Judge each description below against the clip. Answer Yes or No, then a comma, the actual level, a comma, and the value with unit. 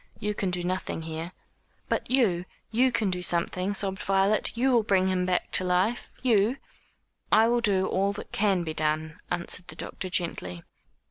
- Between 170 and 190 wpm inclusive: Yes, average, 185 wpm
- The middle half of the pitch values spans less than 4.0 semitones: Yes, average, 3.1 semitones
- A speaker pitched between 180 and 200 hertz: Yes, high, 190 Hz